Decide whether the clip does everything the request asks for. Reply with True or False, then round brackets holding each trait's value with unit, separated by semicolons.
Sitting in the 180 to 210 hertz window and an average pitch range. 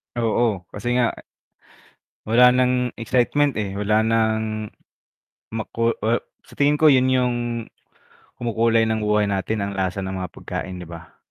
False (115 Hz; 3.2 semitones)